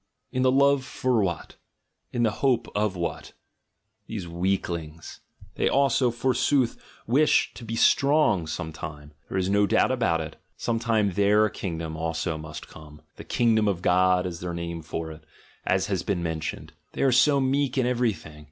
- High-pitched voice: No, low, 100 Hz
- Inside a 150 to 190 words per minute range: Yes, average, 180 wpm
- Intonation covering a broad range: Yes, wide, 6.7 semitones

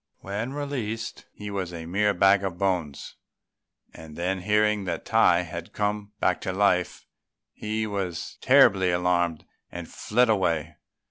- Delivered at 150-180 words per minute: No, average, 140 wpm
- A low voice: Yes, very low, 95 Hz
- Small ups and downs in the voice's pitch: No, average, 3.2 semitones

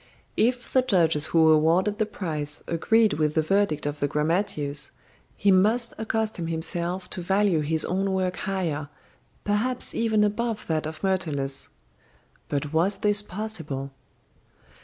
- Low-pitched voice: No, medium, 180 Hz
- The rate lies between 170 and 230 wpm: No, average, 140 wpm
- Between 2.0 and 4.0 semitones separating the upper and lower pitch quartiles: No, average, 5.1 semitones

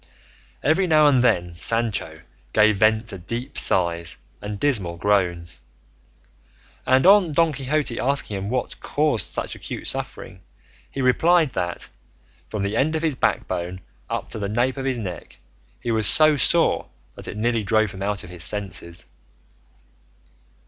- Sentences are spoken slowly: No, average, 155 wpm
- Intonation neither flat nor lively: No, wide, 6.0 semitones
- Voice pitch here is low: Yes, low, 110 Hz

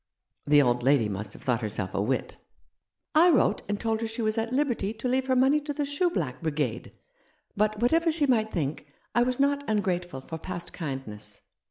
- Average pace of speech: No, fast, 220 wpm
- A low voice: No, high, 210 Hz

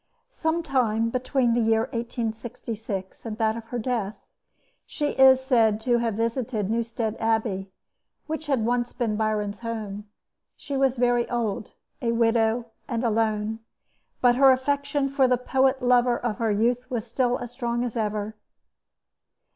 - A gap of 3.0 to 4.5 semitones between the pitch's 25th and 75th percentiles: No, narrow, 2.4 semitones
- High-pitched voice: Yes, high, 235 Hz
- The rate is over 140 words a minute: Yes, average, 150 wpm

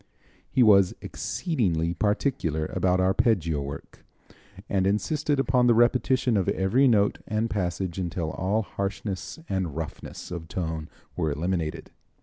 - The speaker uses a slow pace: Yes, slow, 130 wpm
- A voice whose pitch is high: No, very low, 95 Hz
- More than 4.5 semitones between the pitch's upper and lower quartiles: Yes, average, 5.0 semitones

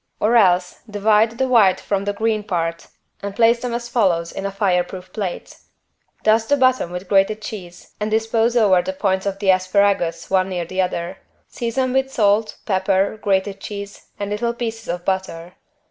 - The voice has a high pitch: Yes, high, 200 Hz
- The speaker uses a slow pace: No, average, 175 wpm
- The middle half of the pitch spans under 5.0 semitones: Yes, average, 3.1 semitones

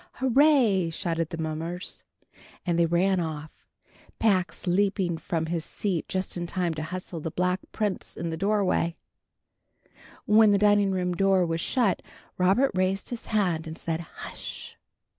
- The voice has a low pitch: No, medium, 180 Hz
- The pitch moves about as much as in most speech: Yes, average, 3.2 semitones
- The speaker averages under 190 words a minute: Yes, average, 150 wpm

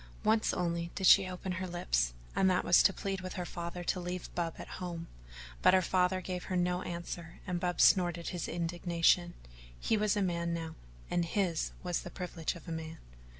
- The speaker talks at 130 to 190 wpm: No, fast, 205 wpm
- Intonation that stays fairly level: Yes, narrow, 1.4 semitones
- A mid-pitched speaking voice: Yes, medium, 175 Hz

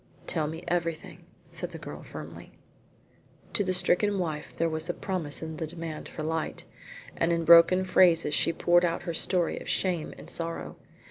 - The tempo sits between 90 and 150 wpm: No, average, 180 wpm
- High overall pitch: No, medium, 170 Hz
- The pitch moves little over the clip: Yes, narrow, 1.7 semitones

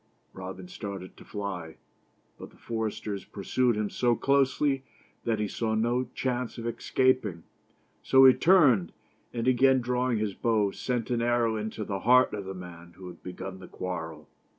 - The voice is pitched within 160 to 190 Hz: No, low, 110 Hz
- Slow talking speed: No, average, 165 wpm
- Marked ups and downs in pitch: No, average, 4.6 semitones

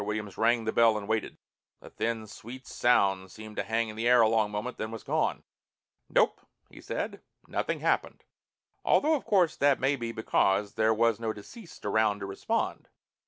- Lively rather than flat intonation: No, narrow, 2.6 semitones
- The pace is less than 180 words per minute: No, average, 185 wpm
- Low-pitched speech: Yes, low, 110 Hz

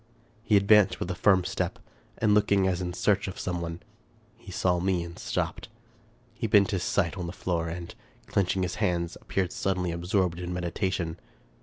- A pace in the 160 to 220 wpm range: Yes, average, 180 wpm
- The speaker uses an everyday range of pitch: No, narrow, 2.2 semitones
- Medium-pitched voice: No, very low, 90 Hz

